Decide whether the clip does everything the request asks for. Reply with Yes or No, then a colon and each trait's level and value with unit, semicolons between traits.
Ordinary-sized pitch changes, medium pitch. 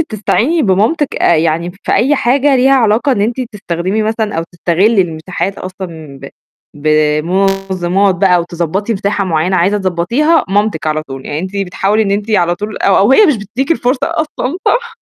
No: average, 4.8 semitones; high, 195 Hz